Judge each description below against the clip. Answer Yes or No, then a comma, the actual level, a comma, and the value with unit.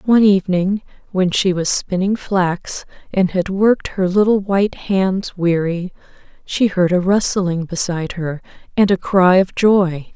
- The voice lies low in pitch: No, medium, 185 Hz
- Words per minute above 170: No, average, 155 wpm